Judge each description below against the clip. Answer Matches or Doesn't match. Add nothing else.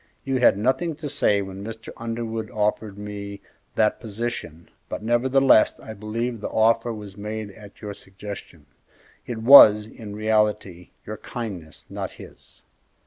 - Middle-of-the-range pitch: Doesn't match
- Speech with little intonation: Matches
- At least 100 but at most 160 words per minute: Matches